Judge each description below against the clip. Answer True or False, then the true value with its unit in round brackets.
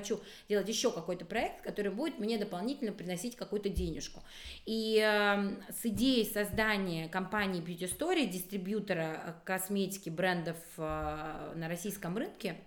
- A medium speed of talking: True (130 wpm)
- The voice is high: True (200 Hz)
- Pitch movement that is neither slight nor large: True (3.2 semitones)